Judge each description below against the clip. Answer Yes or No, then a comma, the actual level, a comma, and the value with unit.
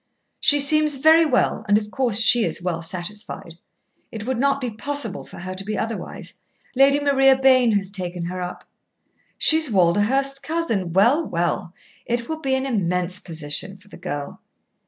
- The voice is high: Yes, high, 220 Hz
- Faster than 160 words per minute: Yes, average, 175 wpm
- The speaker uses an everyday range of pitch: No, wide, 6.9 semitones